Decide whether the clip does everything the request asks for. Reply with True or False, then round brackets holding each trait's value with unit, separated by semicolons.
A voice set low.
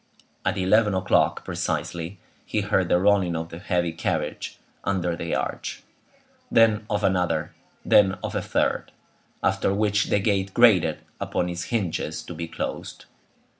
True (95 Hz)